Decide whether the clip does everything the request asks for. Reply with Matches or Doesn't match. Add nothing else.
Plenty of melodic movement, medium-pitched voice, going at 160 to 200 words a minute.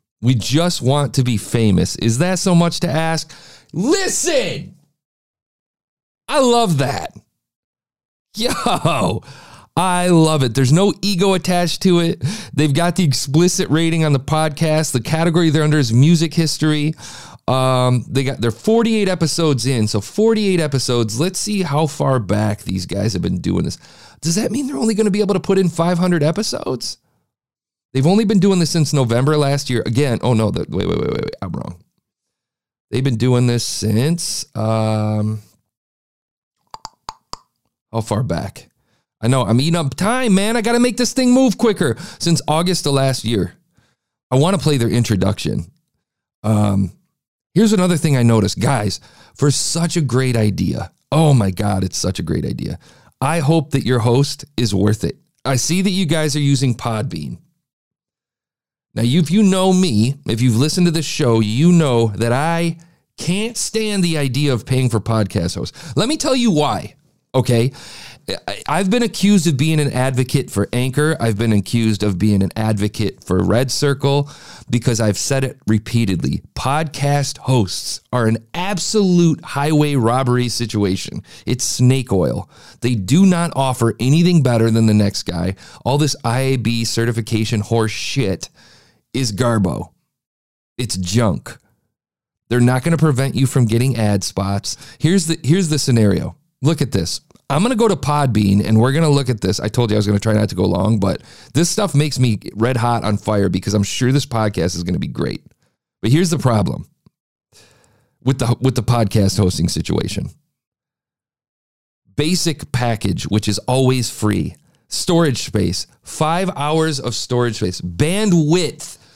Doesn't match